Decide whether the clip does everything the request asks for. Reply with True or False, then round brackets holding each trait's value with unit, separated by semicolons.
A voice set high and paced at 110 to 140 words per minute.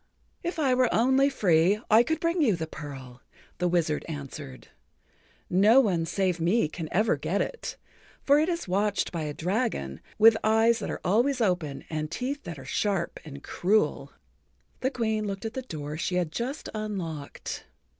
False (195 Hz; 175 wpm)